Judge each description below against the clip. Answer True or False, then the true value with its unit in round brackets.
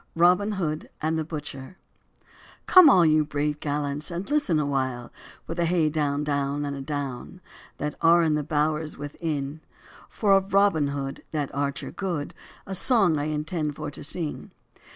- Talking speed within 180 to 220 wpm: False (160 wpm)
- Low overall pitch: False (150 Hz)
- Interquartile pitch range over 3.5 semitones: False (3.1 semitones)